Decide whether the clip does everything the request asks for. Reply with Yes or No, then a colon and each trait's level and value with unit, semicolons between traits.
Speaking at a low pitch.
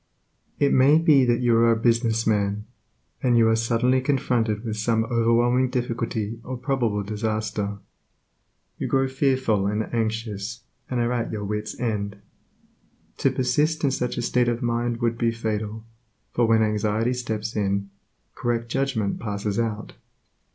Yes: low, 115 Hz